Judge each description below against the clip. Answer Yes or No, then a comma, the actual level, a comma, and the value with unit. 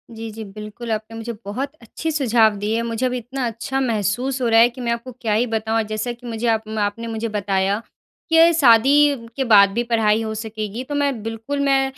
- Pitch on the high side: Yes, high, 230 Hz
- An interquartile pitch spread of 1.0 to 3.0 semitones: Yes, average, 2.7 semitones